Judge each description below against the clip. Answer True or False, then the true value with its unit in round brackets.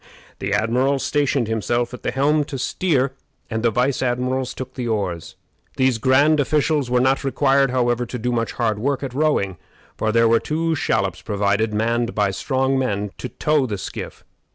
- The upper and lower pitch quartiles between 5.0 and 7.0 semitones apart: False (3.4 semitones)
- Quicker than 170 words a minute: True (180 wpm)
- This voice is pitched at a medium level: False (125 Hz)